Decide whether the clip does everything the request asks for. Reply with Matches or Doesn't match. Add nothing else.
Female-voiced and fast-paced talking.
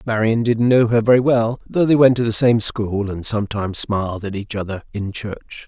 Doesn't match